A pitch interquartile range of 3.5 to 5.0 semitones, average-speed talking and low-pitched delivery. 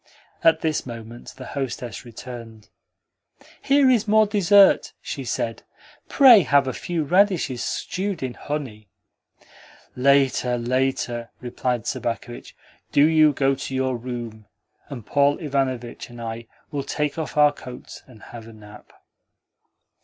No: average, 4.3 semitones; slow, 130 wpm; low, 130 Hz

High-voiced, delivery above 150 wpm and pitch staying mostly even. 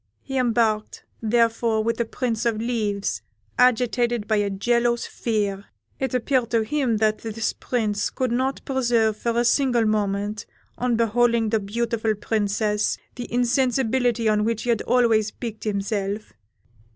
No: high, 230 Hz; average, 145 wpm; narrow, 2.1 semitones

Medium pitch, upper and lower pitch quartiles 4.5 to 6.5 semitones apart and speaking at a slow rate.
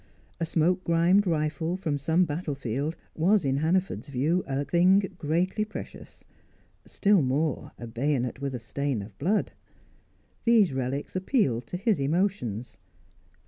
Yes: medium, 160 Hz; average, 5.2 semitones; slow, 130 wpm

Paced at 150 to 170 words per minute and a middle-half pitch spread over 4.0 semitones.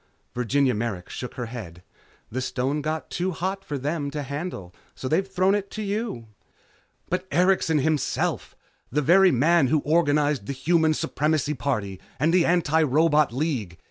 Yes: average, 155 wpm; average, 4.9 semitones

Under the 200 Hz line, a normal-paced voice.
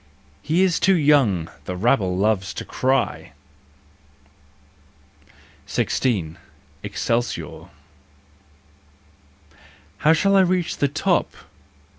No: low, 135 Hz; slow, 100 wpm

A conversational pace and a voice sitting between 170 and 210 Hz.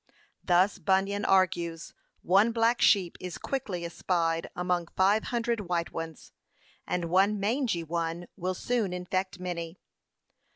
No: slow, 125 wpm; medium, 185 Hz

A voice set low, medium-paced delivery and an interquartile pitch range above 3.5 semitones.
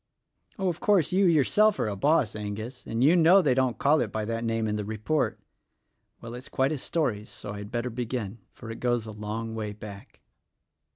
No: low, 120 Hz; fast, 215 wpm; wide, 5.4 semitones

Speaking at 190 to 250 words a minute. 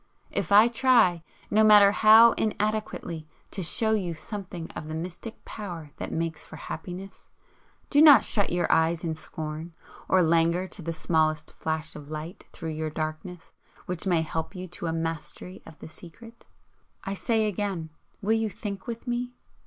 No: average, 170 wpm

